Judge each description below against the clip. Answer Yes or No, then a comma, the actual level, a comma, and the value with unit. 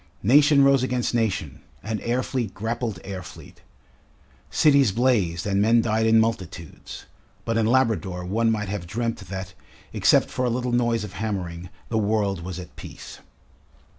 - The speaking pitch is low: Yes, low, 110 Hz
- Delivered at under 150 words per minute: No, average, 160 wpm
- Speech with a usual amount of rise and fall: Yes, average, 3.8 semitones